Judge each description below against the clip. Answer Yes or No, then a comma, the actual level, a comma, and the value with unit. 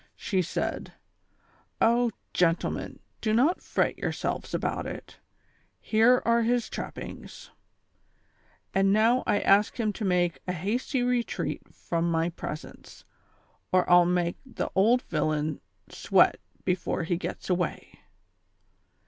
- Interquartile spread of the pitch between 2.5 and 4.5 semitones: No, average, 5.1 semitones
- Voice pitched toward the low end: No, high, 195 Hz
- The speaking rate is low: Yes, slow, 125 wpm